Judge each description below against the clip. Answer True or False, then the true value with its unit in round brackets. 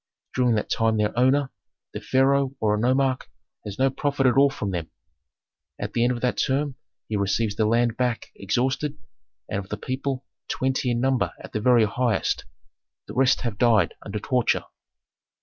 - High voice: False (125 Hz)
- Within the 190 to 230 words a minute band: False (180 wpm)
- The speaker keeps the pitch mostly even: False (3.6 semitones)